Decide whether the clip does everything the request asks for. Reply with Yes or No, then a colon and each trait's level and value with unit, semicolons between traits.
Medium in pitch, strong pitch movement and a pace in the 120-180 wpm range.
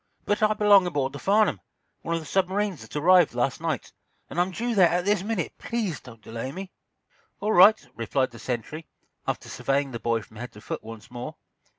No: medium, 165 Hz; wide, 7.8 semitones; fast, 205 wpm